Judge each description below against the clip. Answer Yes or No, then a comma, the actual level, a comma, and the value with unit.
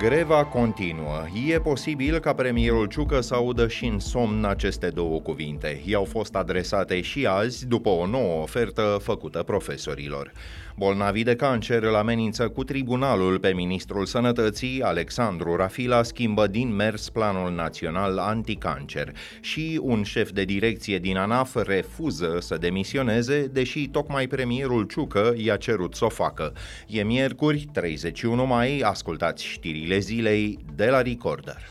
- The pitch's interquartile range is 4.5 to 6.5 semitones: Yes, average, 4.9 semitones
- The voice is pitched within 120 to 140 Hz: No, low, 110 Hz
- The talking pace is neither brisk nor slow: Yes, average, 140 wpm